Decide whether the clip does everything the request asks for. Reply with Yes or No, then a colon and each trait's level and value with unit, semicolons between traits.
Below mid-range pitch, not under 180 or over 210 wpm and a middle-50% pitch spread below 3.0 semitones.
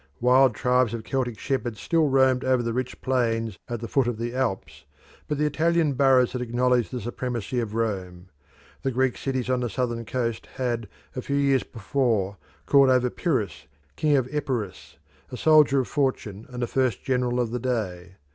Yes: low, 125 Hz; average, 185 wpm; narrow, 2.4 semitones